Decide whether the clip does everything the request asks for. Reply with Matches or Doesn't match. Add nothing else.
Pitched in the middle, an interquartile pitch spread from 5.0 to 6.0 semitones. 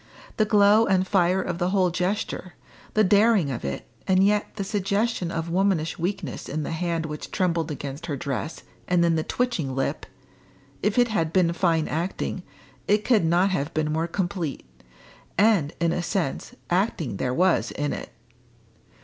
Doesn't match